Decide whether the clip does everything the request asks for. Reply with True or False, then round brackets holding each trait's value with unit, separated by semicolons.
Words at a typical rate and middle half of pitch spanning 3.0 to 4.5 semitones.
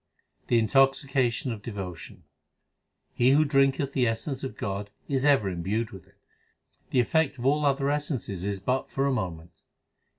False (160 wpm; 5.2 semitones)